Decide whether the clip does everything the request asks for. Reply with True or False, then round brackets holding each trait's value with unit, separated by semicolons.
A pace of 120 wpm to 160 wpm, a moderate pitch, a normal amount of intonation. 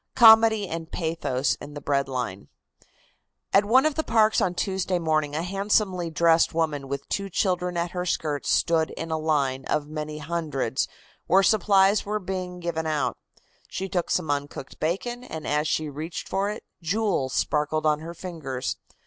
False (170 wpm; 165 Hz; 4.3 semitones)